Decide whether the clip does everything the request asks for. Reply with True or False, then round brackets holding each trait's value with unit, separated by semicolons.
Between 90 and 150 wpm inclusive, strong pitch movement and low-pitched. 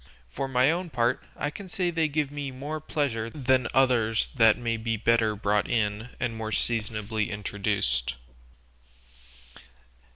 False (140 wpm; 4.2 semitones; 115 Hz)